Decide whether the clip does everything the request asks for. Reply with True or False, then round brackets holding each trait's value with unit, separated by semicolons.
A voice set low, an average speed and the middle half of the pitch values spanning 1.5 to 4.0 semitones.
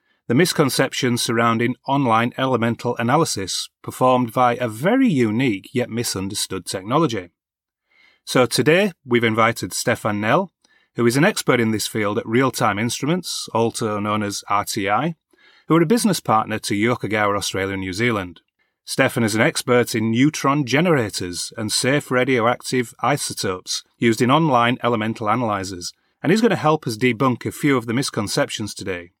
True (120 Hz; 150 wpm; 3.4 semitones)